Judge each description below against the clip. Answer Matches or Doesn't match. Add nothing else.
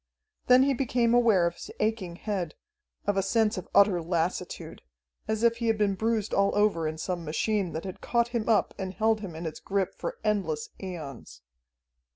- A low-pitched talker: Doesn't match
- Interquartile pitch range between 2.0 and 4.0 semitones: Doesn't match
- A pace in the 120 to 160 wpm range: Doesn't match